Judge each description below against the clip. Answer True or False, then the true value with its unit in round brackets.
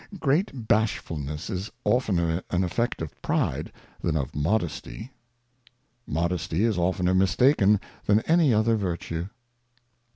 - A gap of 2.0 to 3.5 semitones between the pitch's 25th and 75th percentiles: False (4.9 semitones)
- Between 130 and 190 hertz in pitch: False (95 Hz)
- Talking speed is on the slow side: True (120 wpm)